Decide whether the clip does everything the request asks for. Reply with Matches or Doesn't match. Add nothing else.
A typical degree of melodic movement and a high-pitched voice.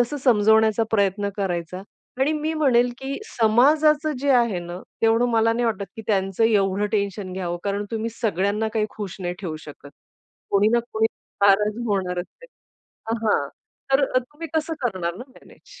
Matches